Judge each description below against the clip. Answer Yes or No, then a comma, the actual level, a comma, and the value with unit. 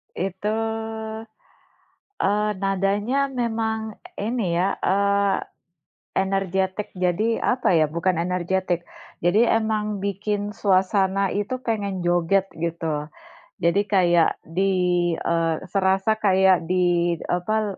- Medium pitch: No, high, 195 Hz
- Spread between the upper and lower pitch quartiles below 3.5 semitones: Yes, average, 2.8 semitones